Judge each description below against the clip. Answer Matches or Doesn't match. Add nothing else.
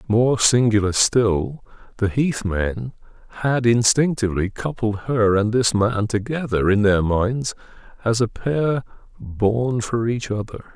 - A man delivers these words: Matches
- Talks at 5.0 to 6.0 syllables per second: Doesn't match